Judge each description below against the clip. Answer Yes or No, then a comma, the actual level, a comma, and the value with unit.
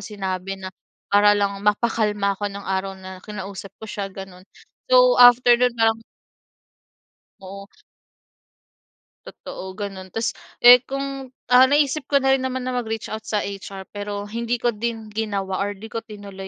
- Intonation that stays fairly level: No, average, 3.4 semitones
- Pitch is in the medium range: No, high, 210 Hz